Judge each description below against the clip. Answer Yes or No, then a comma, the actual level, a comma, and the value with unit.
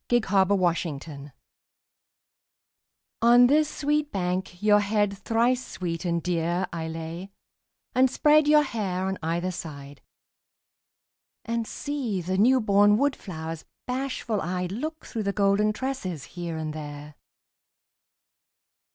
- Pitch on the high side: Yes, high, 195 Hz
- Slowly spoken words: Yes, slow, 120 wpm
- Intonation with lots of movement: Yes, wide, 6.1 semitones